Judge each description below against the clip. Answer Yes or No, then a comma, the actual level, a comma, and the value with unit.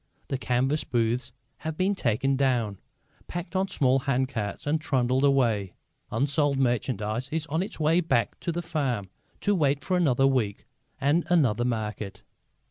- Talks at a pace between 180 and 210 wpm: No, average, 150 wpm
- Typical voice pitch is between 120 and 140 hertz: Yes, low, 135 Hz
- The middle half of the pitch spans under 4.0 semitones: No, average, 4.6 semitones